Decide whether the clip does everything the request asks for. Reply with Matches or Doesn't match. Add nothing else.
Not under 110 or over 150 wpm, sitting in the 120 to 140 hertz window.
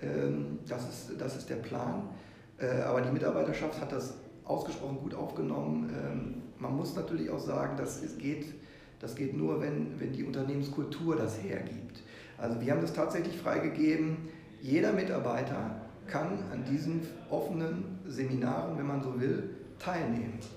Matches